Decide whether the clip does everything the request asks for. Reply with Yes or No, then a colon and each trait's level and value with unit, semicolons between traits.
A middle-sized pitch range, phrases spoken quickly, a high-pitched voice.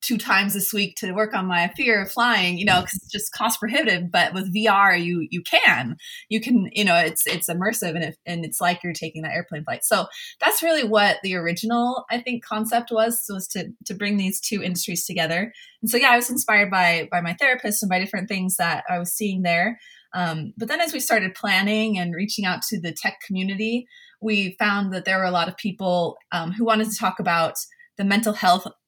Yes: average, 3.8 semitones; fast, 230 wpm; high, 200 Hz